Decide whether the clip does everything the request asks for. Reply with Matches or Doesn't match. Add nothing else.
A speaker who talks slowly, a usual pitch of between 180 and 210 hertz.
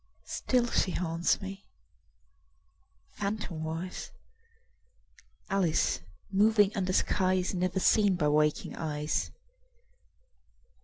Matches